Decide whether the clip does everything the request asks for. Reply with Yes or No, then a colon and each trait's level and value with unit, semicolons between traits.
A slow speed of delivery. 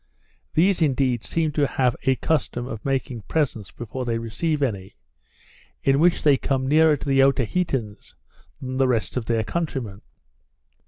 No: average, 155 wpm